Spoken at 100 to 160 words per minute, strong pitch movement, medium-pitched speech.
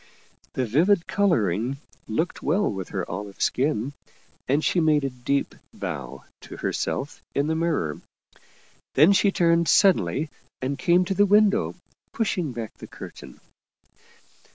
Yes: average, 140 wpm; wide, 7.0 semitones; medium, 150 Hz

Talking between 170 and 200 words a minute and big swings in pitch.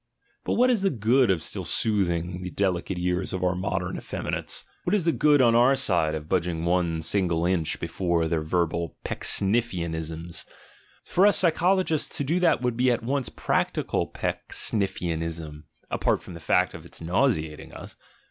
Yes: average, 175 wpm; wide, 6.7 semitones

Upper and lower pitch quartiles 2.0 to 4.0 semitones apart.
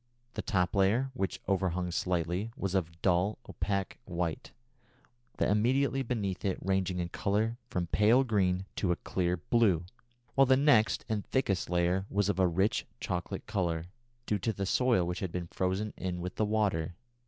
Yes: average, 3.2 semitones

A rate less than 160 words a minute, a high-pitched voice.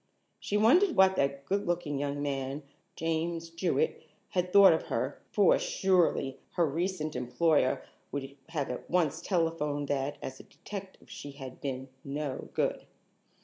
No: average, 145 wpm; medium, 160 Hz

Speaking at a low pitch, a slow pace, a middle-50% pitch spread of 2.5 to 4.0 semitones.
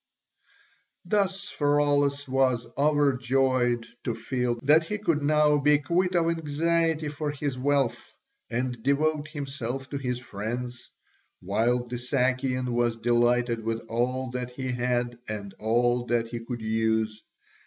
Yes: low, 130 Hz; slow, 130 wpm; average, 3.3 semitones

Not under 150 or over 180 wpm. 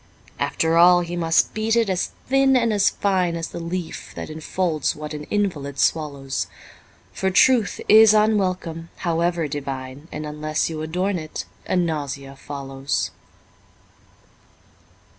No: slow, 135 wpm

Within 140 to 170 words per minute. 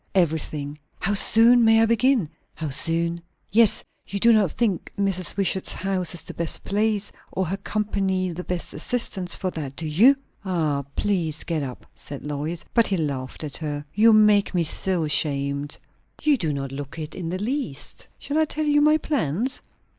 No: average, 180 wpm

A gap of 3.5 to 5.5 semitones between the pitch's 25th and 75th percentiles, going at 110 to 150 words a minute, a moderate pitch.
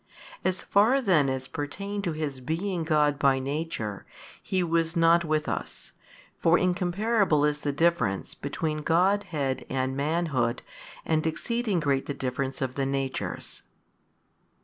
Yes: average, 4.3 semitones; slow, 135 wpm; medium, 155 Hz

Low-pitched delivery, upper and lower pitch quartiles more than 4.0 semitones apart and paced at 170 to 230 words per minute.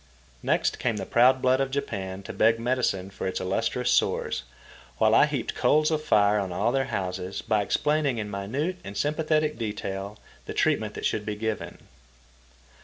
Yes: low, 110 Hz; wide, 5.4 semitones; average, 175 wpm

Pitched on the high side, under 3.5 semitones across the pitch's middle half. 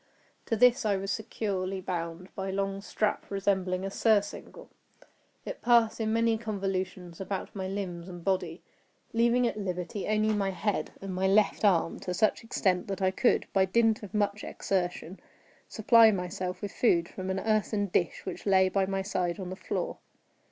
Yes: high, 195 Hz; narrow, 2.5 semitones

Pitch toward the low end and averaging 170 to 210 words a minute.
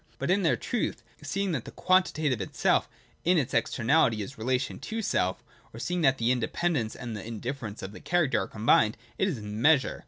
Yes: low, 130 Hz; average, 190 wpm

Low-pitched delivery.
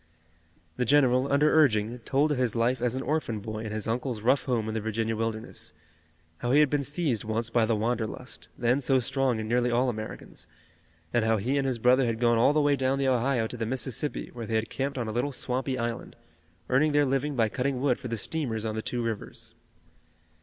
Yes: low, 125 Hz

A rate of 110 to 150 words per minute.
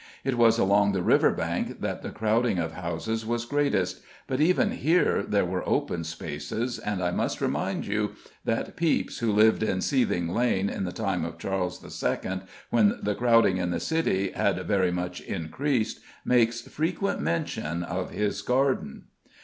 No: average, 165 wpm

